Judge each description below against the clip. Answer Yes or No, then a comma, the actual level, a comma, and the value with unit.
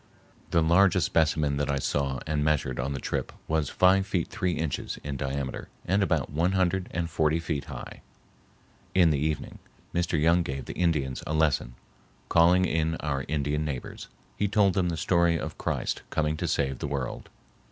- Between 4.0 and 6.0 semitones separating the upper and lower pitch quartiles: No, average, 3.4 semitones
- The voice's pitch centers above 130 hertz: No, very low, 80 Hz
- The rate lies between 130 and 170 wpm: No, average, 180 wpm